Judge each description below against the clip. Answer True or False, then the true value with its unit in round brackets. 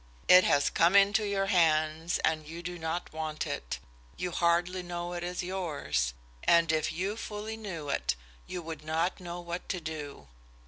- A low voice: False (170 Hz)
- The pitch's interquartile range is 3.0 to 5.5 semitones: False (2.4 semitones)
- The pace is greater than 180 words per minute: False (175 wpm)